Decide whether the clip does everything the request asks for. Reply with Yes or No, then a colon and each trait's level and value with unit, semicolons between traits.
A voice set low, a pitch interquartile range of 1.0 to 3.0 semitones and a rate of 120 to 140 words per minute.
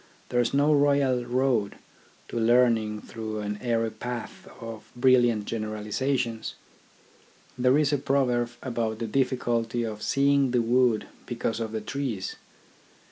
Yes: low, 120 Hz; narrow, 2.6 semitones; slow, 135 wpm